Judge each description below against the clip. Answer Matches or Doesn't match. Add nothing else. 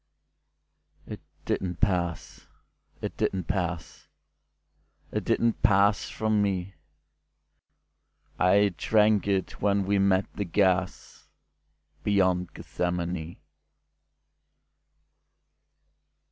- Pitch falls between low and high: Doesn't match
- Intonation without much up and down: Matches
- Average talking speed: Doesn't match